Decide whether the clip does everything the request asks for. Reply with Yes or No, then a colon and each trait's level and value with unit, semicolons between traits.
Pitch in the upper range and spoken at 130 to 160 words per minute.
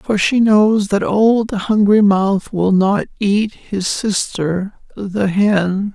Yes: high, 200 Hz; average, 140 wpm